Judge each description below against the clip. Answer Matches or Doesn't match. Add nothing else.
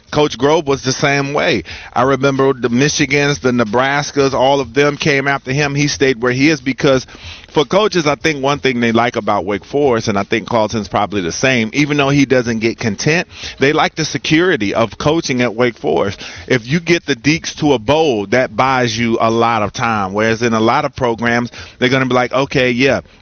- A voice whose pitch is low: Matches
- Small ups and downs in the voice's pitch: Doesn't match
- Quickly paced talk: Matches